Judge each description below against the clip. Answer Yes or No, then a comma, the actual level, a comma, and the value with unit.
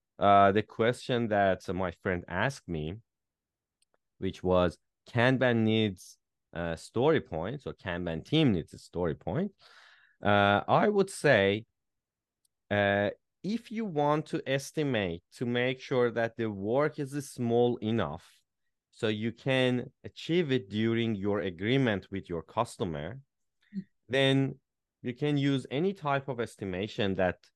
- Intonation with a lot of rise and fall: Yes, wide, 5.7 semitones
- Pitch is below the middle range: Yes, low, 115 Hz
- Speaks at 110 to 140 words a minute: Yes, slow, 135 wpm